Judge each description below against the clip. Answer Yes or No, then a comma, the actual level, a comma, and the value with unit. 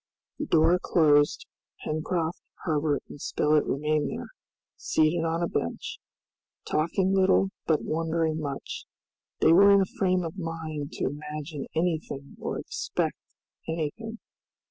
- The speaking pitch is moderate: Yes, medium, 160 Hz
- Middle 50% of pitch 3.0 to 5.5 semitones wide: No, narrow, 2.6 semitones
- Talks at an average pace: No, slow, 125 wpm